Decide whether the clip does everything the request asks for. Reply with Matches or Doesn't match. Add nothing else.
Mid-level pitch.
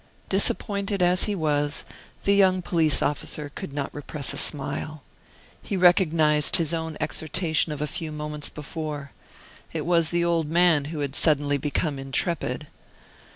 Matches